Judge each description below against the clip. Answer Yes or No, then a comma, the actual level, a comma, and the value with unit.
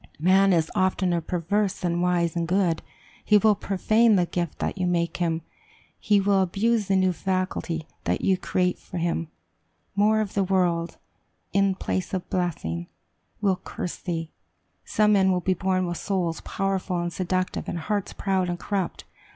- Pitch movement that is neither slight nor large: No, narrow, 2.1 semitones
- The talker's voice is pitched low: No, medium, 185 Hz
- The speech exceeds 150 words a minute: Yes, average, 165 wpm